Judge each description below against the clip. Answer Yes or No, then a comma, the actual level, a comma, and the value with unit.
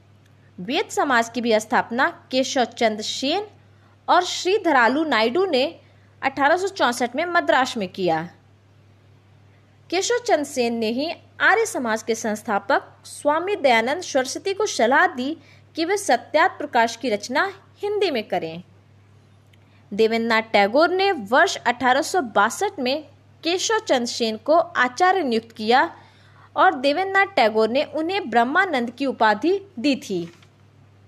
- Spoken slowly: No, average, 125 wpm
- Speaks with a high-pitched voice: Yes, very high, 255 Hz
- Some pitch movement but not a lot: No, wide, 7.6 semitones